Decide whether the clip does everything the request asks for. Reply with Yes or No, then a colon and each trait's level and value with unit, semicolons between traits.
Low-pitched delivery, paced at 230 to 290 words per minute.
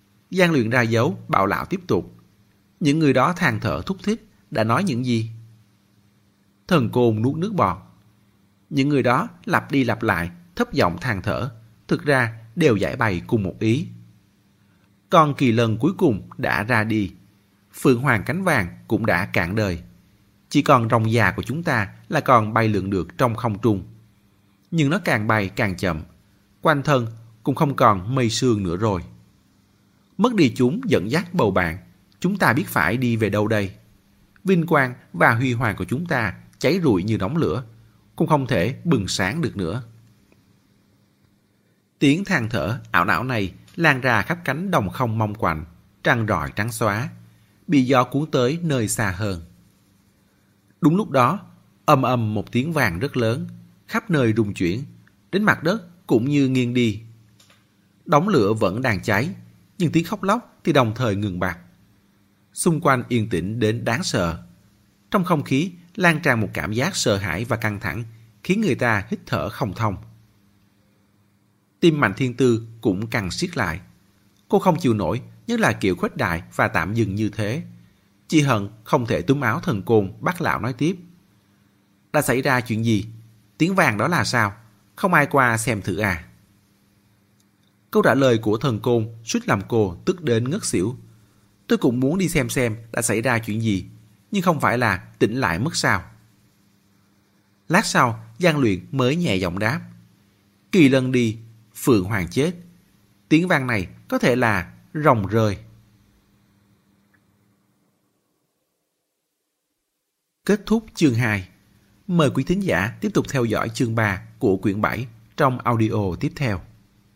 No: low, 110 Hz; average, 170 wpm